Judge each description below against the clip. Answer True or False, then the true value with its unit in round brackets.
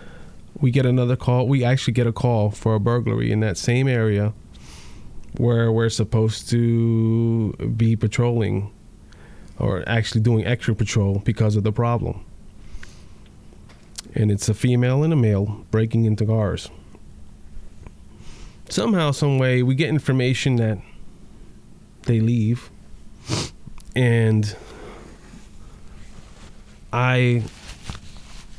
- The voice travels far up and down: False (2.6 semitones)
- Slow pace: True (105 wpm)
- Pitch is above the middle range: False (115 Hz)